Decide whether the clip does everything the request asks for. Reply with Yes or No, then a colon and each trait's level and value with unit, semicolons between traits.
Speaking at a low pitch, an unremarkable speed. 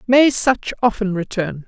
No: high, 215 Hz; average, 145 wpm